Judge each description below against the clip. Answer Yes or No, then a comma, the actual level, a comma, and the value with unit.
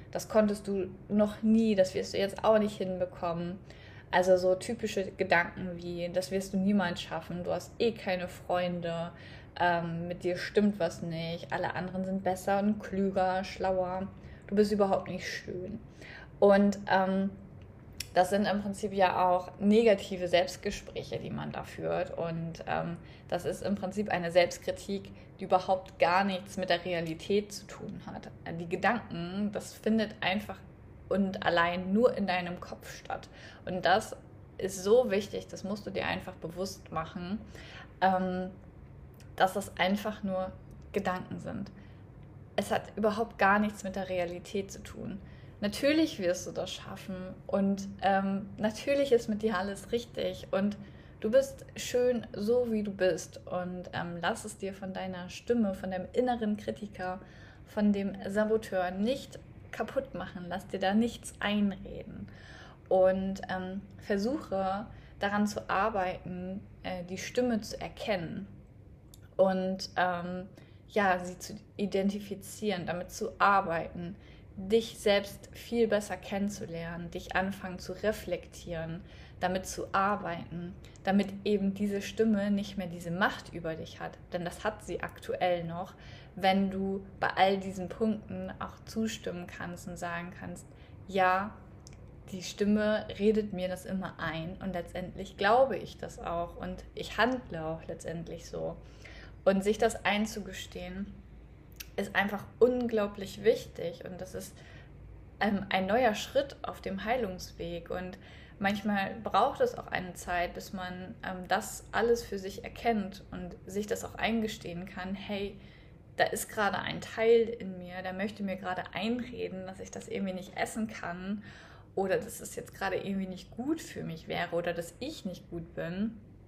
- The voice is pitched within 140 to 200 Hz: Yes, high, 190 Hz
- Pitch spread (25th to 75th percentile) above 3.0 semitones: No, narrow, 2.5 semitones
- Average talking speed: Yes, average, 150 wpm